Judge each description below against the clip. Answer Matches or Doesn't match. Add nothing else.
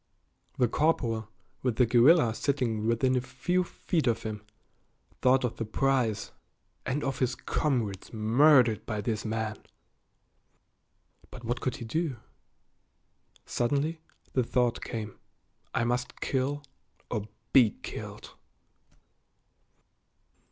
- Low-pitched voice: Matches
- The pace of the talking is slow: Matches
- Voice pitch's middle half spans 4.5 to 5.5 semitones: Doesn't match